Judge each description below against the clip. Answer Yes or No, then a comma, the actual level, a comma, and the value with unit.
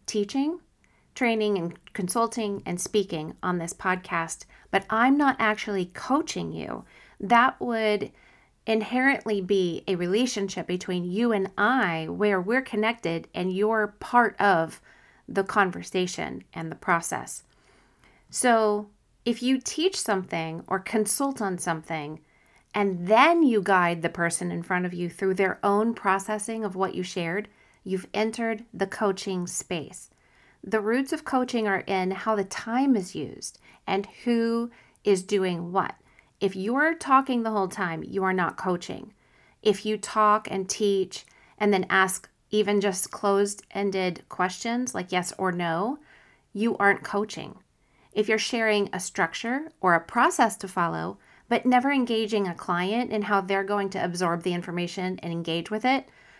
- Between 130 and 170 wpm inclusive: Yes, average, 150 wpm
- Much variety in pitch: No, average, 3.5 semitones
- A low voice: No, high, 200 Hz